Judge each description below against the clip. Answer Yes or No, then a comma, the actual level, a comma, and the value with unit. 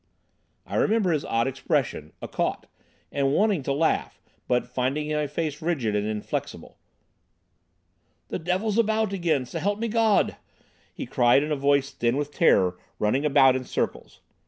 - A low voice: No, medium, 145 Hz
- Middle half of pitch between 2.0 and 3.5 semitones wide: No, wide, 5.4 semitones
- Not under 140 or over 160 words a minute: Yes, average, 155 wpm